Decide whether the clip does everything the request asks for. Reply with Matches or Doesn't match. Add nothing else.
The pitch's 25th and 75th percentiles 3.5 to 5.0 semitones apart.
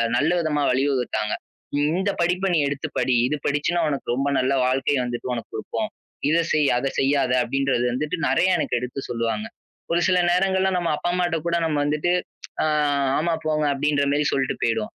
Matches